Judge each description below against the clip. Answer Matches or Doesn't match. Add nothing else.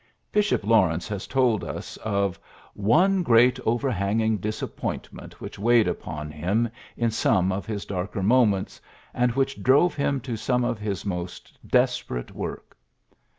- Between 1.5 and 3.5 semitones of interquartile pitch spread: Doesn't match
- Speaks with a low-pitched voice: Matches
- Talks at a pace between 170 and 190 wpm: Doesn't match